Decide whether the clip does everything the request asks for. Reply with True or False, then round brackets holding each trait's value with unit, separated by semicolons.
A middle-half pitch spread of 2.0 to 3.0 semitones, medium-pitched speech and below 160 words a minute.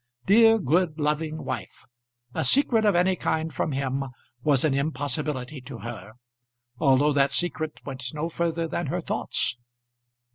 False (3.6 semitones; 150 Hz; 145 wpm)